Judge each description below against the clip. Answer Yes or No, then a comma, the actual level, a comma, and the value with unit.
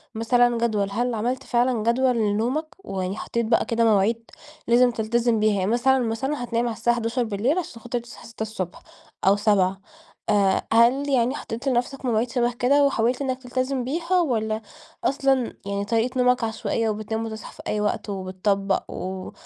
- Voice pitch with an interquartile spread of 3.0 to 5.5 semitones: No, narrow, 2.6 semitones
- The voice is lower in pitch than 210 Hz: No, high, 235 Hz